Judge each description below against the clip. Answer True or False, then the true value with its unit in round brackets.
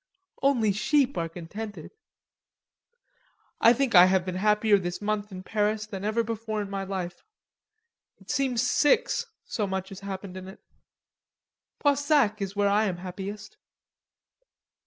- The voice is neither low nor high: False (205 Hz)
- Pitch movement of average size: True (3.0 semitones)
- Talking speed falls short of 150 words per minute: True (140 wpm)